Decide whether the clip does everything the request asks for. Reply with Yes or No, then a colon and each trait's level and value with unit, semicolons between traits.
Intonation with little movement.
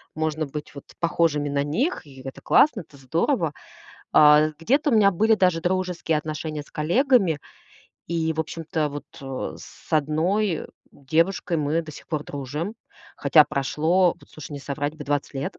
No: average, 3.3 semitones